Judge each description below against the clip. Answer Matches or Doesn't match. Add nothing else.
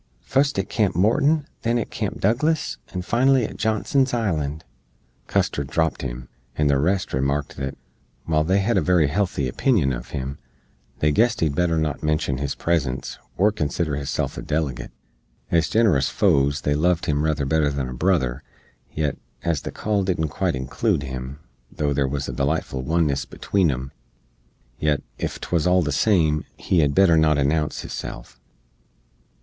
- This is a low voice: Matches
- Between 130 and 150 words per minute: Doesn't match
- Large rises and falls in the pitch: Doesn't match